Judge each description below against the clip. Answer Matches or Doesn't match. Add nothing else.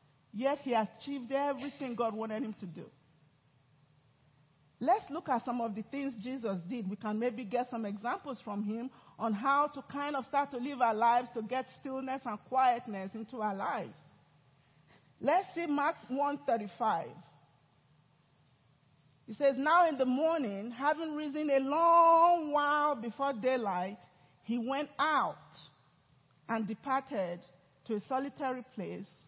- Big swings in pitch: Matches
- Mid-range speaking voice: Doesn't match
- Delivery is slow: Doesn't match